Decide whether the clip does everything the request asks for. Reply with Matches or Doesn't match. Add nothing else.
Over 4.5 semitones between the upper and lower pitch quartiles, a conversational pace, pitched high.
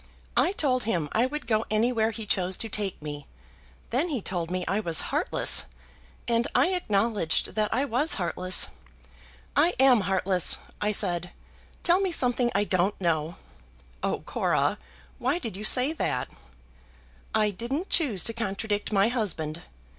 Matches